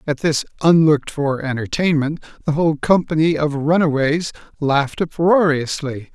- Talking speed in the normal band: No, slow, 115 wpm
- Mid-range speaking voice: Yes, medium, 150 Hz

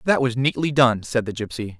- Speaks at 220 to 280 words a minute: Yes, fast, 235 wpm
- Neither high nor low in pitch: No, low, 120 Hz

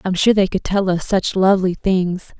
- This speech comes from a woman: Yes, female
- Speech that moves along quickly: Yes, fast, 225 wpm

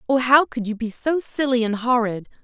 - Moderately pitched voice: No, high, 245 Hz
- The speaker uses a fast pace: Yes, fast, 220 wpm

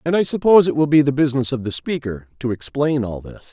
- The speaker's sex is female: No, male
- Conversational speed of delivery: No, fast, 255 wpm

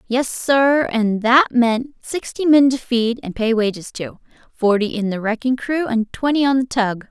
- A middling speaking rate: Yes, average, 185 wpm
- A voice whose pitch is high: Yes, high, 245 Hz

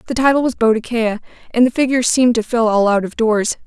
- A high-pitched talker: Yes, high, 235 Hz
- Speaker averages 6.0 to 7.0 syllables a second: Yes, 6.4 syllables/s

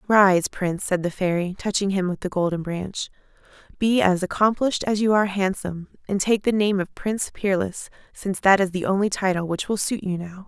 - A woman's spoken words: Yes, female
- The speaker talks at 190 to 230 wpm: Yes, fast, 205 wpm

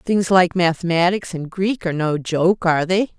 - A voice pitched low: No, medium, 175 Hz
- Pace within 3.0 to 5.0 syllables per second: Yes, 4.9 syllables/s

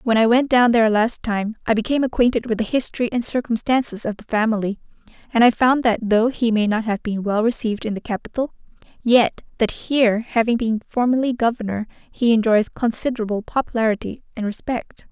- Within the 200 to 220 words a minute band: No, average, 185 wpm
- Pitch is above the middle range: Yes, high, 230 Hz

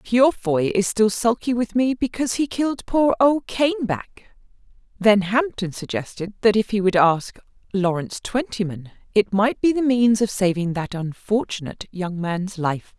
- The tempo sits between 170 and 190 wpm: No, average, 155 wpm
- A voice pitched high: Yes, high, 215 Hz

